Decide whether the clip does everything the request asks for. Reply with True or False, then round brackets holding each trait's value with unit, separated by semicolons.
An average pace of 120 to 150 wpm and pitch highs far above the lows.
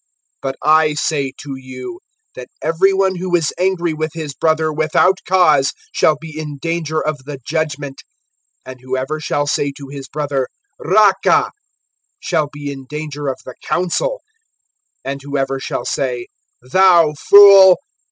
False (145 wpm; 3.7 semitones)